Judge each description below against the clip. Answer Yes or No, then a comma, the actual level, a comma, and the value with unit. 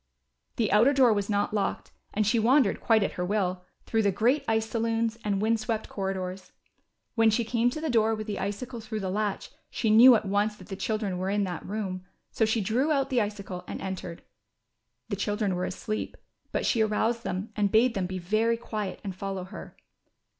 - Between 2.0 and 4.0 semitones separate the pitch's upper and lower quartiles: Yes, average, 2.7 semitones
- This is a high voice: Yes, high, 215 Hz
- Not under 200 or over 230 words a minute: Yes, fast, 205 wpm